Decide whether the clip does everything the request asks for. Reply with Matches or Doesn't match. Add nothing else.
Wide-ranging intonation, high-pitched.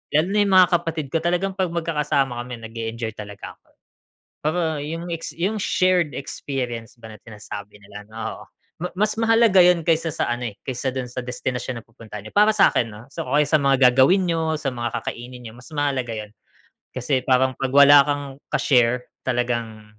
Doesn't match